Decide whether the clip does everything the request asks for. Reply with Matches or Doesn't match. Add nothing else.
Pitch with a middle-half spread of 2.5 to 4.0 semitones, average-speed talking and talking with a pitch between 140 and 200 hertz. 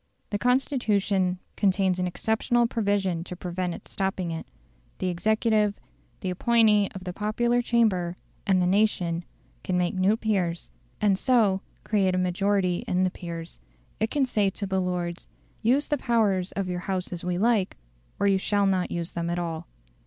Matches